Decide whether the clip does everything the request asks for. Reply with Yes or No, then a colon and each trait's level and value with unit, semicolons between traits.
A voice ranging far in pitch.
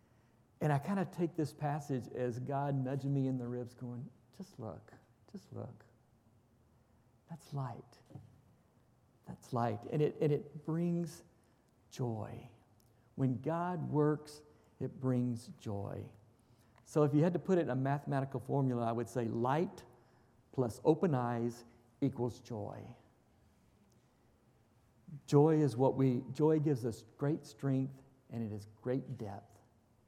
No: average, 3.6 semitones